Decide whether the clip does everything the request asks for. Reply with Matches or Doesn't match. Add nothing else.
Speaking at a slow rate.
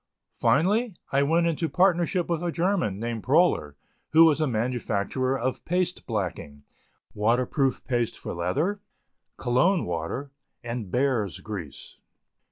Matches